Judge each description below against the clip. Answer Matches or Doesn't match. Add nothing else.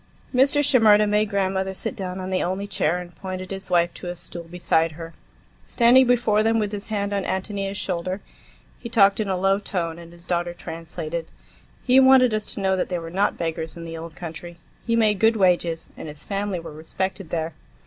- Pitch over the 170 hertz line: Matches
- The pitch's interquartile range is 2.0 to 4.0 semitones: Matches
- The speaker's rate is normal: Doesn't match